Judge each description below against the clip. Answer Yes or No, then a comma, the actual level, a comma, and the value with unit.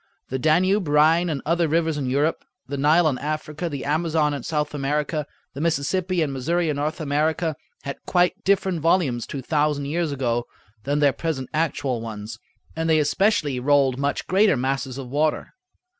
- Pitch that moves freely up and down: No, average, 2.9 semitones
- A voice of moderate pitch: Yes, medium, 150 Hz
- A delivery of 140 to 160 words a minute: No, average, 175 wpm